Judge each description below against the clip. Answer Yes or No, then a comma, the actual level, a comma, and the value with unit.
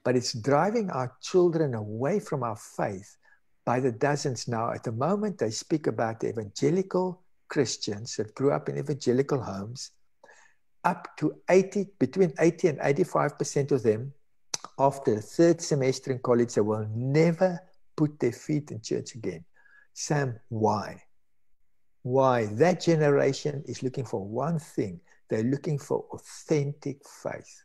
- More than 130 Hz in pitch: Yes, medium, 140 Hz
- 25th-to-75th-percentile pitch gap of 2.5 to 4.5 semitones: No, wide, 5.4 semitones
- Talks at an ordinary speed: Yes, average, 145 wpm